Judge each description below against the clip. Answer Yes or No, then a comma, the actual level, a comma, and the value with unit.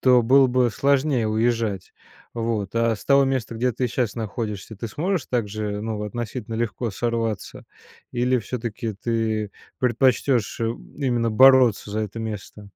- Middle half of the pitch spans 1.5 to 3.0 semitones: Yes, average, 2.7 semitones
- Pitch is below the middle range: Yes, low, 115 Hz